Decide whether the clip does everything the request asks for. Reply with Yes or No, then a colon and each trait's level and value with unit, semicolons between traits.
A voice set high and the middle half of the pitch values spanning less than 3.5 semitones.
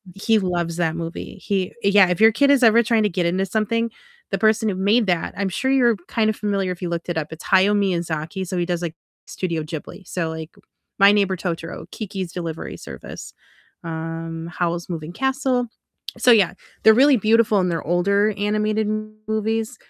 No: high, 195 Hz; average, 4.2 semitones